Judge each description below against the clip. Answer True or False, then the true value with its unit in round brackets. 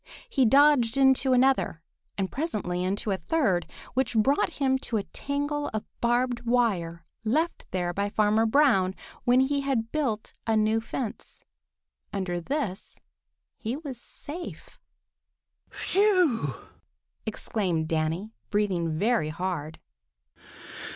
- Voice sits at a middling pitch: False (225 Hz)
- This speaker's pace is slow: True (115 wpm)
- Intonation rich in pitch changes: True (6.2 semitones)